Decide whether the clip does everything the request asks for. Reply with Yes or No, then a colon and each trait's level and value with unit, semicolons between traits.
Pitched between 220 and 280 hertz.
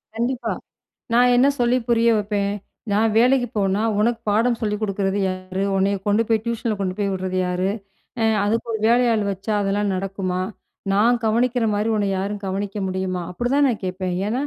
No: high, 210 Hz